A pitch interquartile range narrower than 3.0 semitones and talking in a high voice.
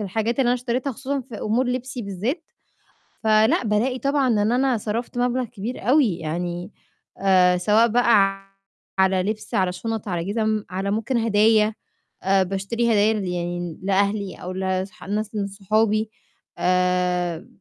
No: average, 3.7 semitones; high, 210 Hz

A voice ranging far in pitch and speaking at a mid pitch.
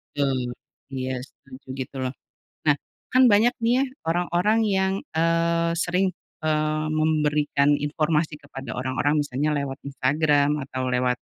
No: average, 3.6 semitones; medium, 150 Hz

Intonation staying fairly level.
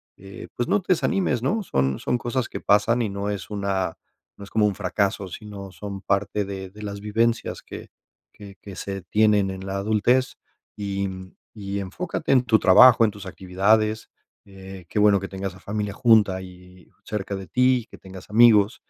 Yes: narrow, 2.3 semitones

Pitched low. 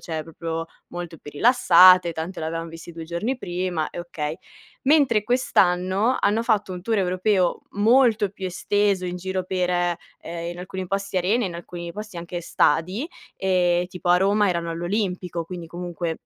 No: medium, 180 Hz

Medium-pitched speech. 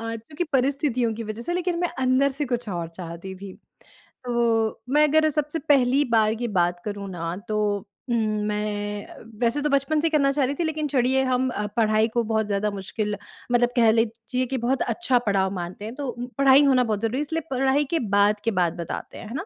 No: high, 235 Hz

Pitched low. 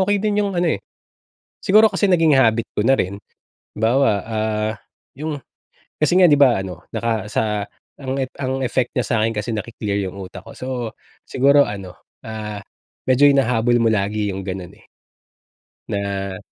Yes: low, 115 Hz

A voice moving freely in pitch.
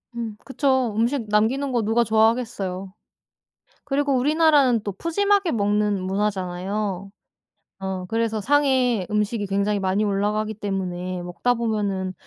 No: average, 4.0 semitones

